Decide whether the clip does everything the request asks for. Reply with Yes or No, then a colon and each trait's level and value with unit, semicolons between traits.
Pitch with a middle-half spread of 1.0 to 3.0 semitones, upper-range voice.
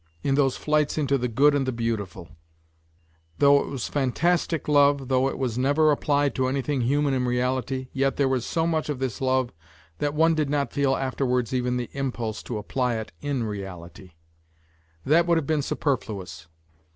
No: average, 2.7 semitones; low, 135 Hz